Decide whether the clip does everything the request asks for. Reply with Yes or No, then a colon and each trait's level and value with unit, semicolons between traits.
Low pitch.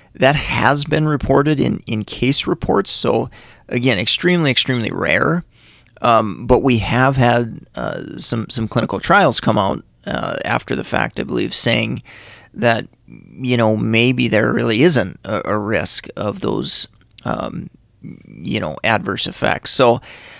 Yes: low, 125 Hz